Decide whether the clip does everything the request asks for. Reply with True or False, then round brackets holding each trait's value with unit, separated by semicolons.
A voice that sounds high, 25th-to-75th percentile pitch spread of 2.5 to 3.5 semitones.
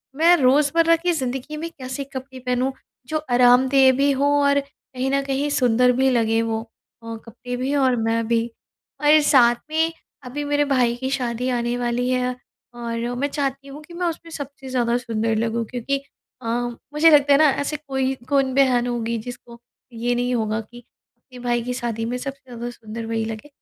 True (255 Hz; 2.8 semitones)